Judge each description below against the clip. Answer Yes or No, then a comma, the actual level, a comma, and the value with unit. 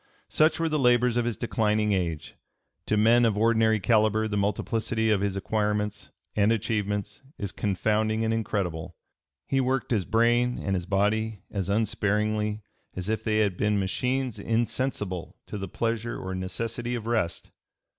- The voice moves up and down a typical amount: No, narrow, 2.3 semitones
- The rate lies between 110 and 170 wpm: Yes, average, 155 wpm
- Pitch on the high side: No, low, 110 Hz